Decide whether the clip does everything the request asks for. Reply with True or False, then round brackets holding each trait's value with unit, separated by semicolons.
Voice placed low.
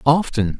True (130 Hz)